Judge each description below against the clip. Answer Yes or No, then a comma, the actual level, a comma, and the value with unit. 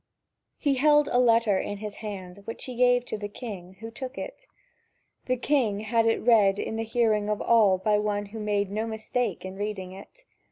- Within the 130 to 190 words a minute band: No, average, 200 wpm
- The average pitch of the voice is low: No, high, 220 Hz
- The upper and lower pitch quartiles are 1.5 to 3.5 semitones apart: Yes, average, 3.1 semitones